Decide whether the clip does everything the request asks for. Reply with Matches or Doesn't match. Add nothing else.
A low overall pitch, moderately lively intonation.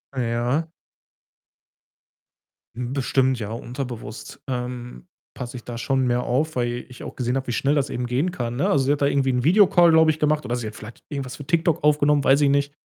Matches